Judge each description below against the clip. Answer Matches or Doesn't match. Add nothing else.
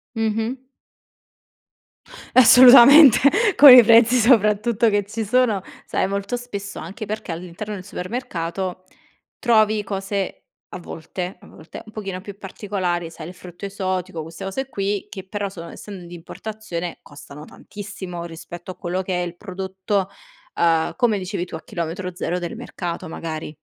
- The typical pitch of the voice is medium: Doesn't match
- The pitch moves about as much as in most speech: Matches